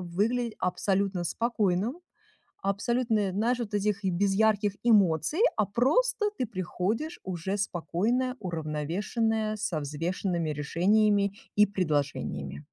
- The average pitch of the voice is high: Yes, high, 200 Hz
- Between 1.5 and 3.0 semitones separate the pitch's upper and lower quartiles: No, average, 4.3 semitones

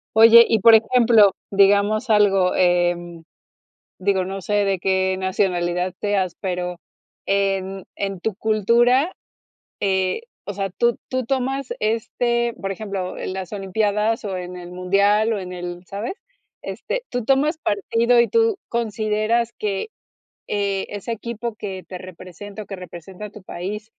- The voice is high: Yes, high, 205 Hz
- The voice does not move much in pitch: No, average, 3.3 semitones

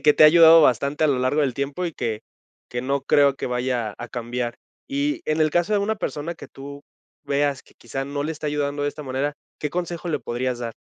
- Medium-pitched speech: Yes, medium, 145 Hz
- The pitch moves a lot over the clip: No, average, 3.3 semitones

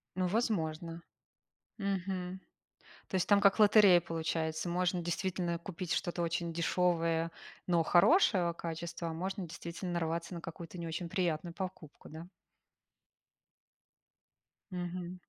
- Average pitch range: No, narrow, 1.8 semitones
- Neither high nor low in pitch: Yes, medium, 175 Hz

